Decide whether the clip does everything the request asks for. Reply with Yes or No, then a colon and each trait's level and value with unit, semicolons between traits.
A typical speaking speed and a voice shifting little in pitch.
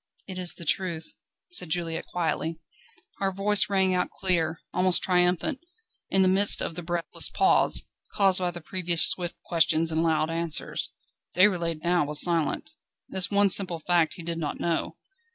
Yes: average, 165 wpm; narrow, 2.2 semitones